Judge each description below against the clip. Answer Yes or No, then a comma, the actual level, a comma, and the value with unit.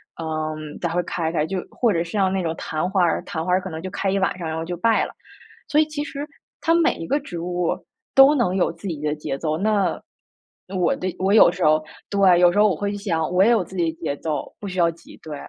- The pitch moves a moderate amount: Yes, average, 3.6 semitones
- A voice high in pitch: No, medium, 180 Hz